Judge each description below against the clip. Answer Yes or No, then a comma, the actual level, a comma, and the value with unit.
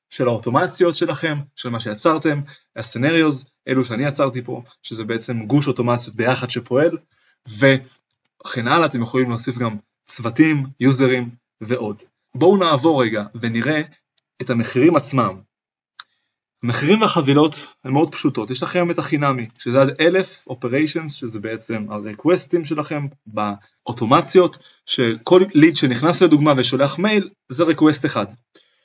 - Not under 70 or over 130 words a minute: Yes, average, 125 wpm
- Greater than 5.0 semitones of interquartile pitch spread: No, average, 4.7 semitones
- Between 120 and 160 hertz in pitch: Yes, low, 135 Hz